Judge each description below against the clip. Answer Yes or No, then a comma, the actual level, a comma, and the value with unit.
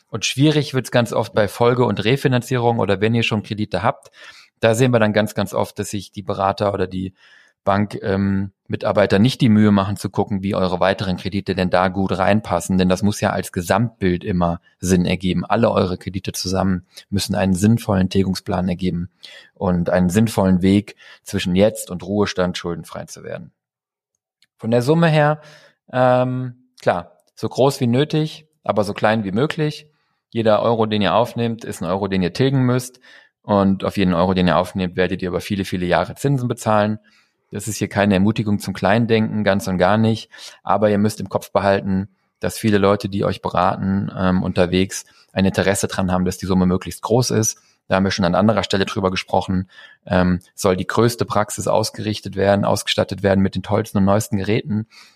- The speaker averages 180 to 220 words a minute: Yes, fast, 190 wpm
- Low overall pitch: Yes, low, 100 Hz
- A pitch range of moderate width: Yes, average, 3.0 semitones